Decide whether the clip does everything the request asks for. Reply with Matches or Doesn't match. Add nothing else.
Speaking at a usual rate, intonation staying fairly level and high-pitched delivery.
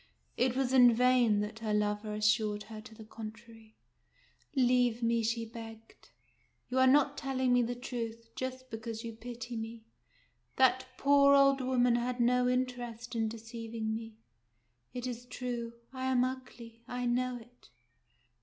Matches